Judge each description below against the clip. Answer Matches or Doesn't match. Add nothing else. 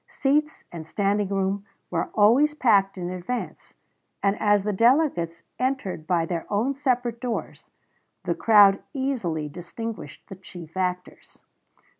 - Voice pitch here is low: Doesn't match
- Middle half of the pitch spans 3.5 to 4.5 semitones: Doesn't match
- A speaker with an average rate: Doesn't match